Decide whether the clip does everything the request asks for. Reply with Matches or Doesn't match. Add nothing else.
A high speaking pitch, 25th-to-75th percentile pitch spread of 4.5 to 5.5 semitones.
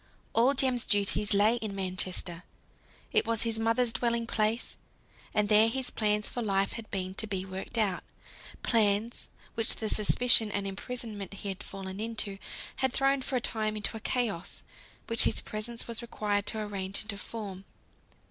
Doesn't match